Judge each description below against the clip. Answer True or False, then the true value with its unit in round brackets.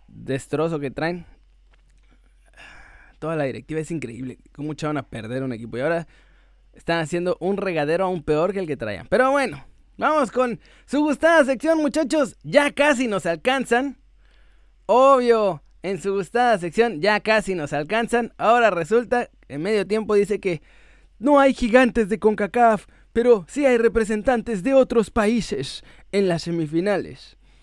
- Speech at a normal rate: True (150 wpm)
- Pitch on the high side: True (210 Hz)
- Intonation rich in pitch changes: True (6.6 semitones)